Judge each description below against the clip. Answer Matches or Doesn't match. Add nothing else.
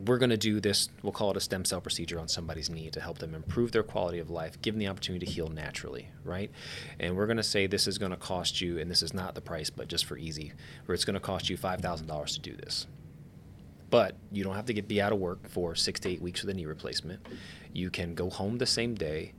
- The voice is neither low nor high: Doesn't match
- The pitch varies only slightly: Doesn't match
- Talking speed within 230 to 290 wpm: Matches